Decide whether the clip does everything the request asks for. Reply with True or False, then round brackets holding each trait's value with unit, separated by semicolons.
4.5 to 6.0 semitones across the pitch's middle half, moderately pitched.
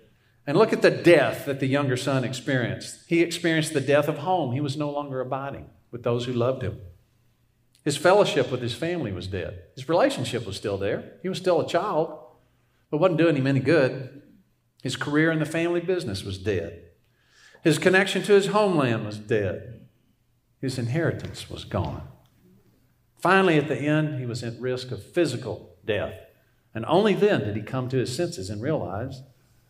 False (5.5 semitones; 130 Hz)